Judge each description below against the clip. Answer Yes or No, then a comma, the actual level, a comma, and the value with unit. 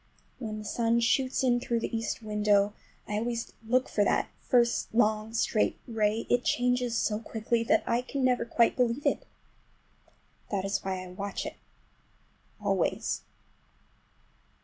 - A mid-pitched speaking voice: No, high, 230 Hz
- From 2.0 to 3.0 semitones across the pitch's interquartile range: Yes, narrow, 2.4 semitones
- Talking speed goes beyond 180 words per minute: No, average, 140 wpm